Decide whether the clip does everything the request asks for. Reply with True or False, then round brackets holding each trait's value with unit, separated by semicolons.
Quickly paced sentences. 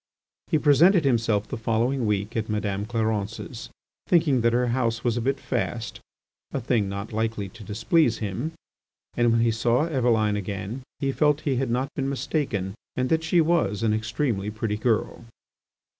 False (160 wpm)